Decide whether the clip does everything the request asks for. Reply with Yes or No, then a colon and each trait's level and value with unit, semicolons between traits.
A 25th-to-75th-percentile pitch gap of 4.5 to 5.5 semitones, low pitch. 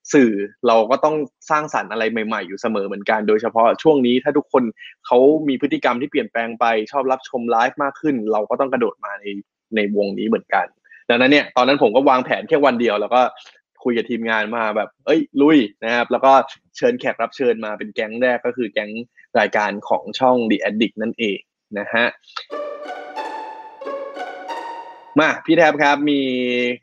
Yes: average, 4.8 semitones; low, 125 Hz